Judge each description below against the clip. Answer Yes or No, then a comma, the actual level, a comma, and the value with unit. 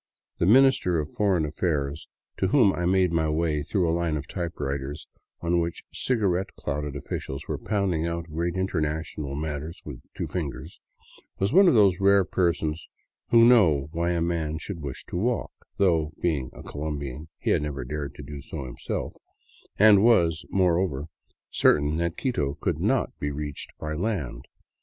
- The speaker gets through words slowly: No, average, 165 wpm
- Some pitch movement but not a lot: Yes, average, 4.0 semitones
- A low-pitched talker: Yes, very low, 80 Hz